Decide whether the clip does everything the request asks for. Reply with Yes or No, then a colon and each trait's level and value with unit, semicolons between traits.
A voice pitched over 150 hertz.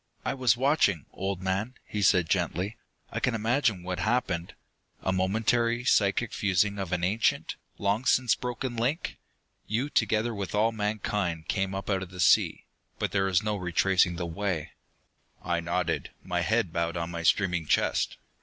No: low, 100 Hz